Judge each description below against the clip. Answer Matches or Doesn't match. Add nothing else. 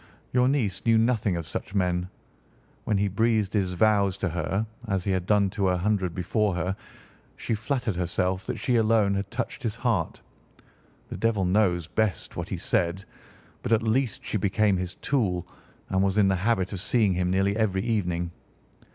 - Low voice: Matches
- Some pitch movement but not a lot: Matches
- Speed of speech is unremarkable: Matches